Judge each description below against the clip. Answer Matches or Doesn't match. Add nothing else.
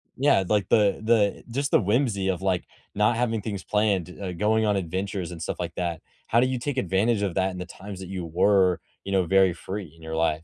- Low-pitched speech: Matches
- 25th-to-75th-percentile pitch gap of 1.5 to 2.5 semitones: Doesn't match